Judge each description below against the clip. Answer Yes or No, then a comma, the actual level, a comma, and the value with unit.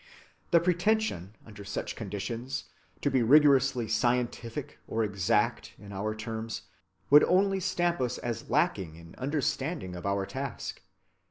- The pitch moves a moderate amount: No, wide, 6.0 semitones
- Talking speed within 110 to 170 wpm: Yes, slow, 135 wpm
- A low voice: Yes, low, 120 Hz